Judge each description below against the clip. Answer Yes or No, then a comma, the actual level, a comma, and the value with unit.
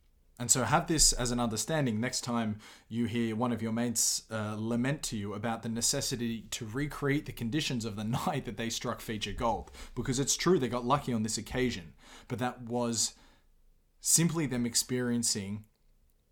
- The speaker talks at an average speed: Yes, average, 180 wpm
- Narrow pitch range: Yes, narrow, 2.2 semitones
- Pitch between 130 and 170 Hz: No, low, 120 Hz